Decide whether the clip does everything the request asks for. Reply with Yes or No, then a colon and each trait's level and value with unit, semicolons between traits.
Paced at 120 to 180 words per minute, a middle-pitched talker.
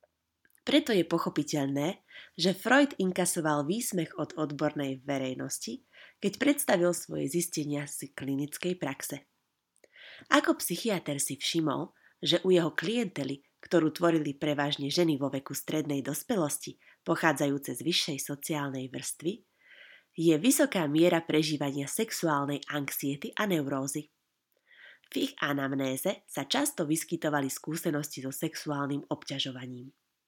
No: slow, 110 wpm; medium, 155 Hz